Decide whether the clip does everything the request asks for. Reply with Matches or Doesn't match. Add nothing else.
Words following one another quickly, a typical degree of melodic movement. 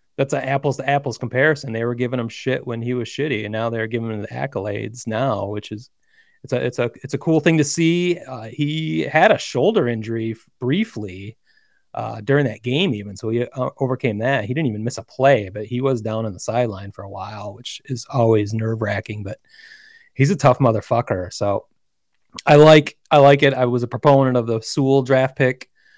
Matches